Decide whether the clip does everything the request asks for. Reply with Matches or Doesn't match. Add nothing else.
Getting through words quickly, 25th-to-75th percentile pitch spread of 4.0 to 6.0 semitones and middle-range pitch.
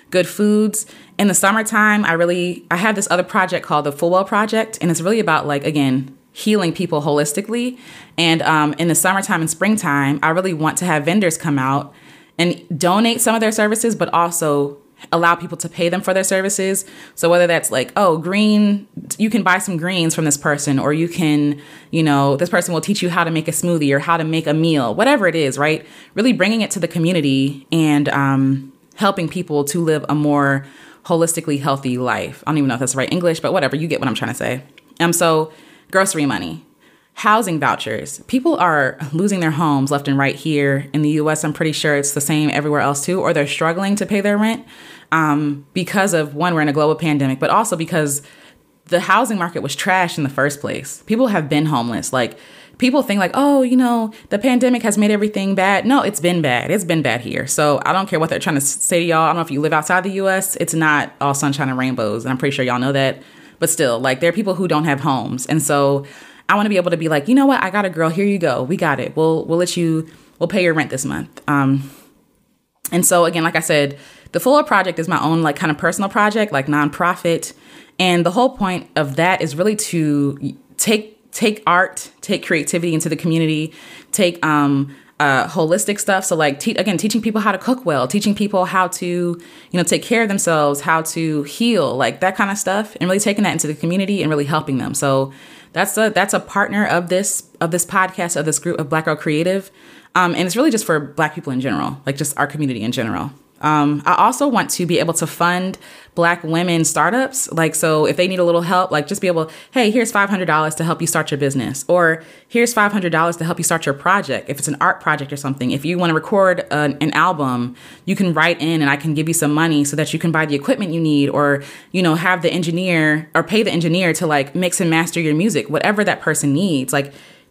Matches